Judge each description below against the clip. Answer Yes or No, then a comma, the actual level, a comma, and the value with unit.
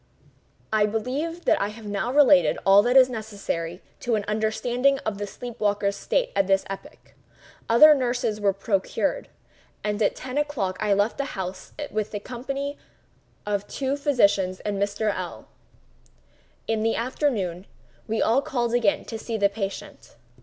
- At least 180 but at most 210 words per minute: No, average, 160 wpm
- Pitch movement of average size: Yes, average, 4.0 semitones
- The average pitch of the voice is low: No, high, 220 Hz